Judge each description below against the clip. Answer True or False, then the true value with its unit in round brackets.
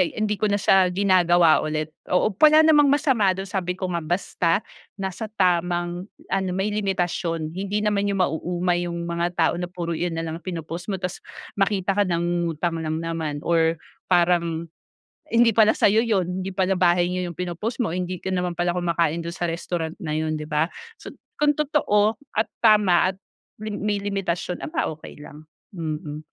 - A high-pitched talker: False (180 Hz)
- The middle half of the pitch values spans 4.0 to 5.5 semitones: False (2.9 semitones)